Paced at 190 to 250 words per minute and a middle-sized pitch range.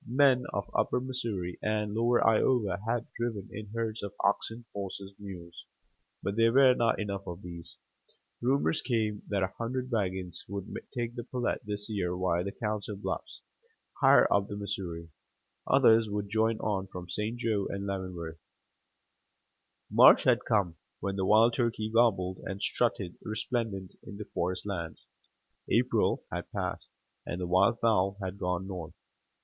No: average, 155 wpm; average, 3.5 semitones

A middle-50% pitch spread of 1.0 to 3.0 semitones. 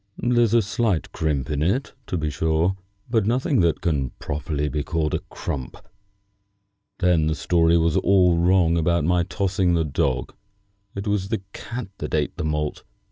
No: average, 4.2 semitones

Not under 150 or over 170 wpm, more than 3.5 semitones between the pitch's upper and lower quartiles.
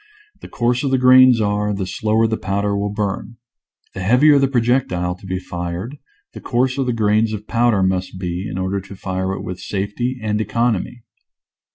No: average, 185 wpm; average, 4.1 semitones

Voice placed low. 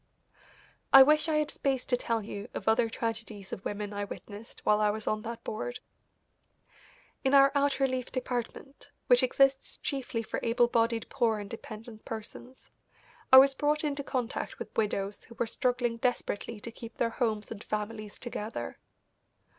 No: high, 235 Hz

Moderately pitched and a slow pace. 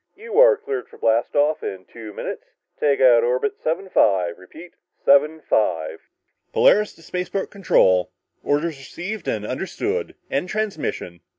Yes: medium, 150 Hz; slow, 130 wpm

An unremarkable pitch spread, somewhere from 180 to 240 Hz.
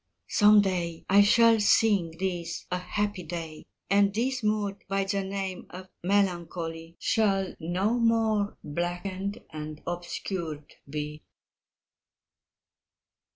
Yes: average, 3.3 semitones; high, 190 Hz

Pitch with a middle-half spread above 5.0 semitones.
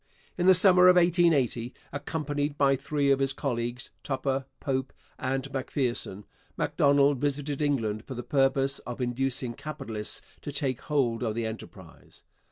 No: average, 2.8 semitones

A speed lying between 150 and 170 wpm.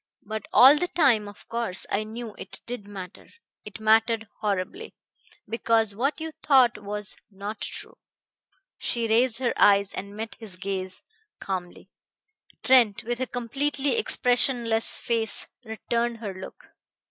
No: slow, 135 wpm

